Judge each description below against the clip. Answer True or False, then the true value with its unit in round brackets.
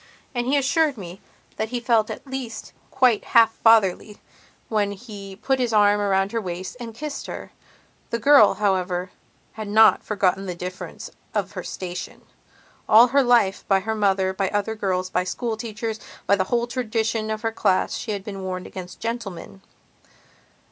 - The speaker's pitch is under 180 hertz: False (215 Hz)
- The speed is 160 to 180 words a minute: True (170 wpm)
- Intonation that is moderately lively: True (3.4 semitones)